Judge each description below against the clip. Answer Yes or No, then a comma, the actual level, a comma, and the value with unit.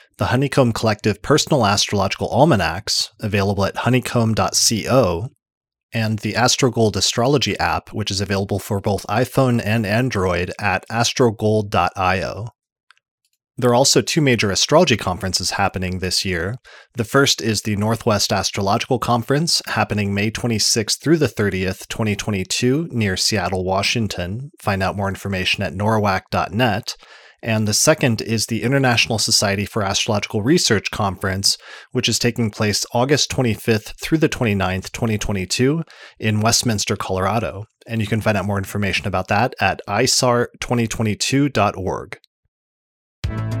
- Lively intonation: No, average, 3.4 semitones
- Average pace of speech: No, slow, 125 wpm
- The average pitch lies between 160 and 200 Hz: No, low, 110 Hz